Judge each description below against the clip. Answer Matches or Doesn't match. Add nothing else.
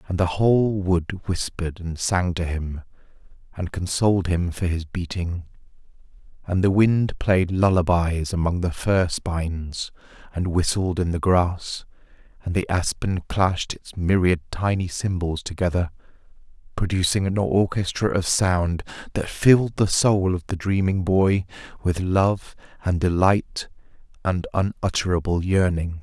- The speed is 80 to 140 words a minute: Matches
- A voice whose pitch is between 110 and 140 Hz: Doesn't match